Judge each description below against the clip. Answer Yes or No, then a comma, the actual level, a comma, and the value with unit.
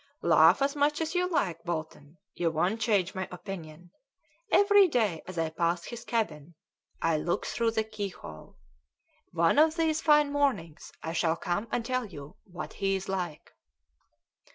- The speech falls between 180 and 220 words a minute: No, average, 155 wpm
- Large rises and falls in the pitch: Yes, wide, 7.2 semitones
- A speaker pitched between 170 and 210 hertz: Yes, high, 190 Hz